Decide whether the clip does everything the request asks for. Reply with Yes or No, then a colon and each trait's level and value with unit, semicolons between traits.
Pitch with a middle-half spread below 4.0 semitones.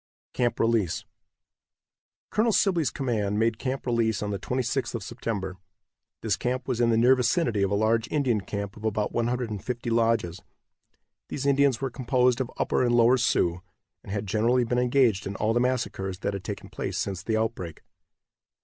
Yes: average, 3.3 semitones